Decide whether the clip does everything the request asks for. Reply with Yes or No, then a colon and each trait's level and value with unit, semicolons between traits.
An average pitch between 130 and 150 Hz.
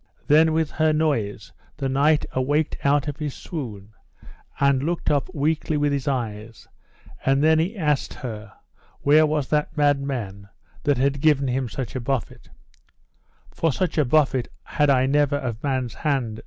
Yes: medium, 140 Hz